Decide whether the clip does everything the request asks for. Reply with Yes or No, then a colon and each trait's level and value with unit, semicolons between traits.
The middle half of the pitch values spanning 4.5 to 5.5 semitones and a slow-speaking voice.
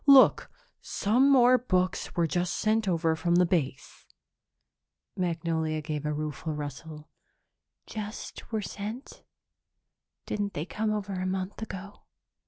Yes: average, 4.9 semitones; slow, 120 wpm